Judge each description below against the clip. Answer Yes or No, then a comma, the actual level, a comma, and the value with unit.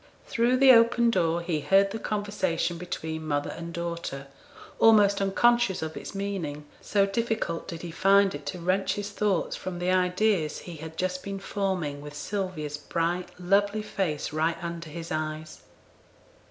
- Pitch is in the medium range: Yes, medium, 180 Hz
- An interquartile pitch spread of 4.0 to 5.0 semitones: No, average, 3.6 semitones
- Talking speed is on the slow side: No, average, 160 wpm